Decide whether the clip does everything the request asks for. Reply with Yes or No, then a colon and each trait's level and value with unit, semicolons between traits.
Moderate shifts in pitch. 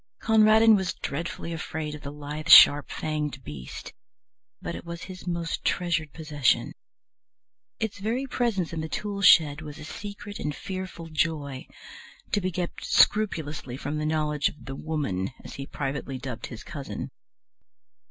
Yes: average, 4.2 semitones